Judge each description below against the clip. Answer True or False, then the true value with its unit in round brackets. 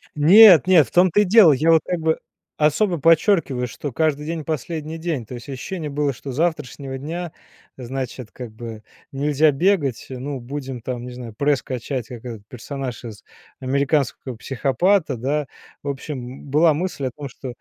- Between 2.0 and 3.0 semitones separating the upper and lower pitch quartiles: False (4.0 semitones)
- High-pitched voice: False (140 Hz)